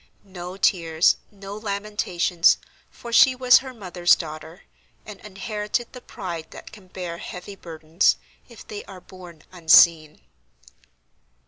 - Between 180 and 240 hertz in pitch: Yes, medium, 185 Hz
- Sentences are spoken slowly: Yes, slow, 125 wpm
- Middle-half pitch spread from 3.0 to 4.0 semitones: Yes, average, 3.7 semitones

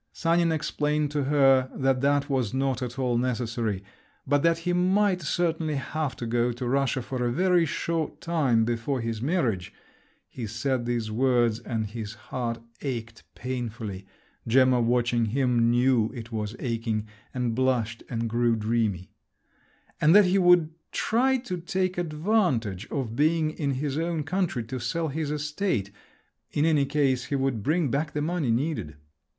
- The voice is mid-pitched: No, low, 130 Hz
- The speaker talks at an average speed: Yes, average, 155 wpm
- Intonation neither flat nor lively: Yes, average, 4.9 semitones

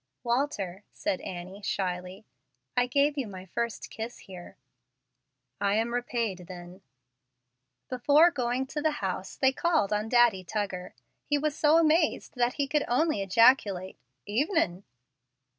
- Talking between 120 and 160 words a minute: Yes, slow, 135 wpm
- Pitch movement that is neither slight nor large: No, wide, 6.8 semitones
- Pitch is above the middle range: Yes, high, 235 Hz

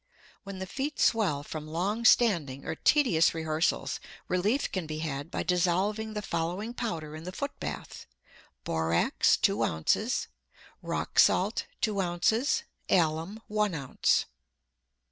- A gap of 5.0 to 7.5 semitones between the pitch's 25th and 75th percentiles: Yes, average, 5.3 semitones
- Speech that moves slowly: Yes, slow, 130 wpm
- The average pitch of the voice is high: No, medium, 180 Hz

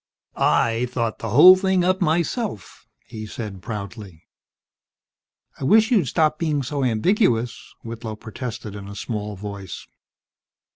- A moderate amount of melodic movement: No, wide, 7.3 semitones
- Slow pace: Yes, slow, 130 wpm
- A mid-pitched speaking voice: No, low, 115 Hz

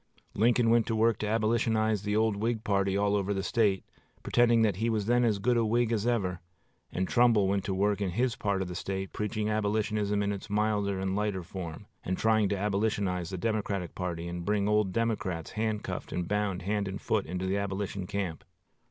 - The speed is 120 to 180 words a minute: No, fast, 205 wpm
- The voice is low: Yes, low, 105 Hz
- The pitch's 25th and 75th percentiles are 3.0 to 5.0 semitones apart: No, narrow, 2.4 semitones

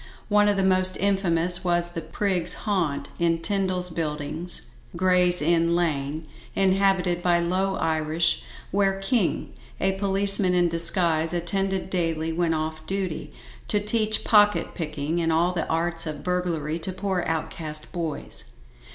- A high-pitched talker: No, medium, 175 Hz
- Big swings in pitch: No, average, 2.8 semitones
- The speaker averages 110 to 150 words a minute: Yes, average, 140 wpm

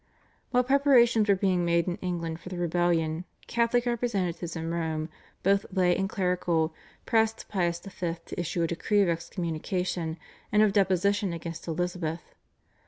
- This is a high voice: No, medium, 180 Hz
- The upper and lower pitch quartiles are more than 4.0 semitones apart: No, average, 3.1 semitones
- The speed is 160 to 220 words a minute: No, average, 150 wpm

